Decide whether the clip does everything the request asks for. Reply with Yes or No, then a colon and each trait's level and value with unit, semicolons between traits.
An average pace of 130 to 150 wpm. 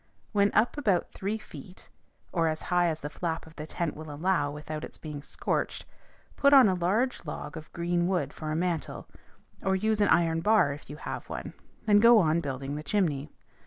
No: average, 200 wpm